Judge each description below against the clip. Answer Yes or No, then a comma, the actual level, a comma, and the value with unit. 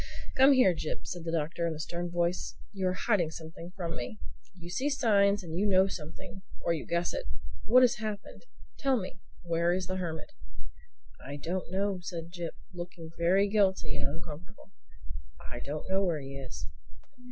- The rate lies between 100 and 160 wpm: No, average, 175 wpm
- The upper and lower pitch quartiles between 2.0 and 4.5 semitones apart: Yes, average, 3.3 semitones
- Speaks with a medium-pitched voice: Yes, medium, 175 Hz